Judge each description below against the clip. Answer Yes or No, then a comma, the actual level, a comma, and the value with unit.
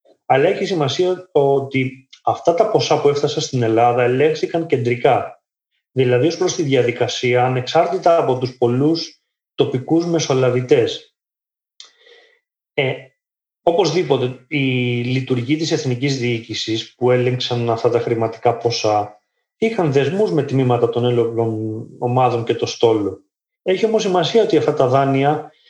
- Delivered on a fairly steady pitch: No, average, 5.1 semitones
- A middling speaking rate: Yes, average, 125 wpm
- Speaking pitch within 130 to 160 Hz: Yes, low, 135 Hz